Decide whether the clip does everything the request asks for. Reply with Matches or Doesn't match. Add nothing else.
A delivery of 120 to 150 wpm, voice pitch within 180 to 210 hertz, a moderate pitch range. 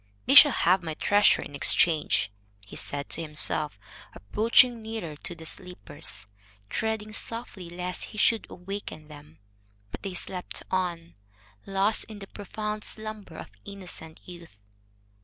Matches